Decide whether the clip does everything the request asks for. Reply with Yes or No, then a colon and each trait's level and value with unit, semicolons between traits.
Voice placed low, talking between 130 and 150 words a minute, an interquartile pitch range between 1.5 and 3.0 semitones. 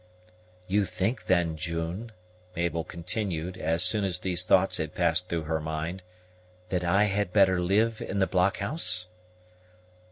Yes: very low, 90 Hz; average, 140 wpm; average, 2.7 semitones